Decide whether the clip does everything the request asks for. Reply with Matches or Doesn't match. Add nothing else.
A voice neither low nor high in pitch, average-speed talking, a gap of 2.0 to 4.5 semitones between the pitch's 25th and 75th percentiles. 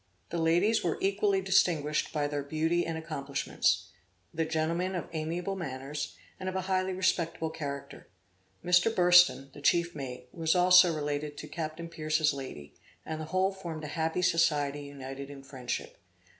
Matches